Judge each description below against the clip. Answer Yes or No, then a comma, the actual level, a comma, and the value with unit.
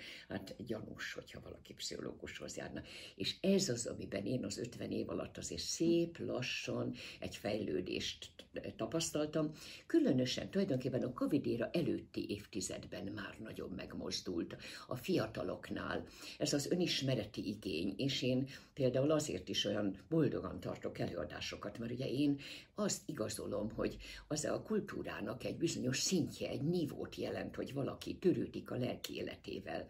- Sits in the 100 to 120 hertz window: No, low, 130 Hz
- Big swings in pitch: Yes, wide, 6.5 semitones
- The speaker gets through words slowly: No, average, 130 wpm